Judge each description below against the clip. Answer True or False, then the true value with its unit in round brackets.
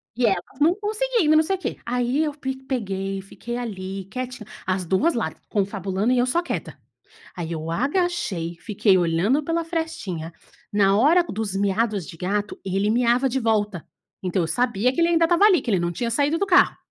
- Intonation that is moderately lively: False (7.6 semitones)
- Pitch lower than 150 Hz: False (230 Hz)